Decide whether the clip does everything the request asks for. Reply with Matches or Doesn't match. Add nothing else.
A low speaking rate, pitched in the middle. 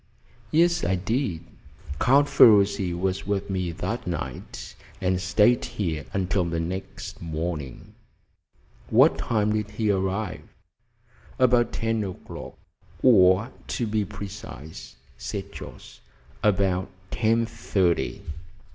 Doesn't match